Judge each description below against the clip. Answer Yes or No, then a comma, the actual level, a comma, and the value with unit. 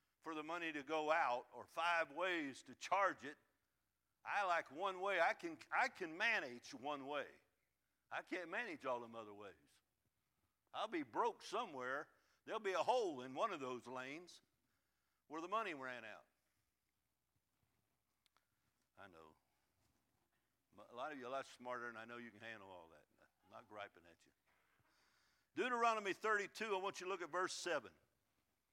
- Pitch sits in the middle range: Yes, medium, 155 Hz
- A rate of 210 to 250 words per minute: No, average, 170 wpm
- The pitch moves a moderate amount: No, wide, 9.0 semitones